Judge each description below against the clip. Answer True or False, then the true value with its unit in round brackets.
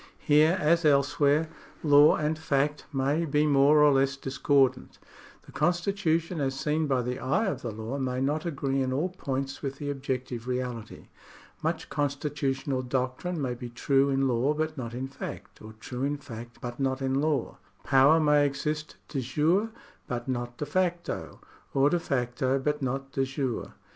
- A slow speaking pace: False (170 wpm)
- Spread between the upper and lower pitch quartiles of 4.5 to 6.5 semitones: False (2.5 semitones)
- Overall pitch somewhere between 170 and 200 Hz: False (140 Hz)